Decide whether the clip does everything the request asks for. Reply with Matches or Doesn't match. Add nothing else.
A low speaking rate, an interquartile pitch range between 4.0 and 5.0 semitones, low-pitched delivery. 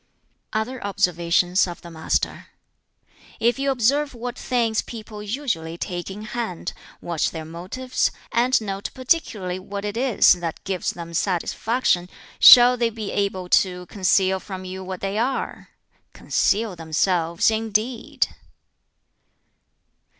Doesn't match